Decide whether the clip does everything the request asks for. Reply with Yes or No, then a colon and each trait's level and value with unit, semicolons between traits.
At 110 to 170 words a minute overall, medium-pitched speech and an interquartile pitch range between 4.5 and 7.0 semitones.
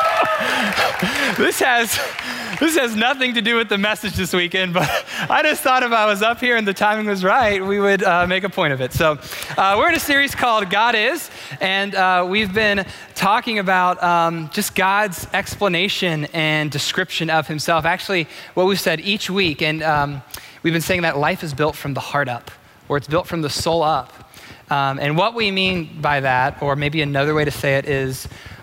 No: fast, 205 wpm; medium, 180 Hz; average, 5.1 semitones